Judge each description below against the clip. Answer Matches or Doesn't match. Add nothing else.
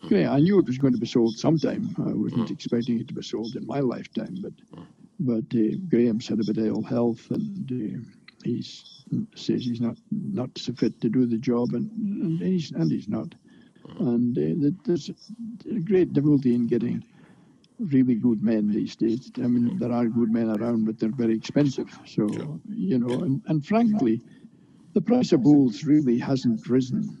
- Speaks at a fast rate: Doesn't match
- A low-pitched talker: Matches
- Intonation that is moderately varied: Doesn't match